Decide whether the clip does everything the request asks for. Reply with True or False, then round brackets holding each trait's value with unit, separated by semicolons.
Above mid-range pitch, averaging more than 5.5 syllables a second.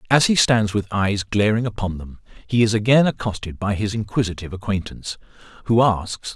False (105 Hz; 5.7 syllables/s)